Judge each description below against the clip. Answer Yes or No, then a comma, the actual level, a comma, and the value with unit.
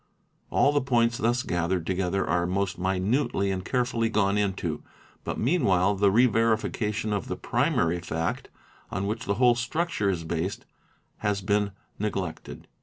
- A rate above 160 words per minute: No, average, 155 wpm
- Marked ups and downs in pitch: No, average, 3.8 semitones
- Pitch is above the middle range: No, low, 100 Hz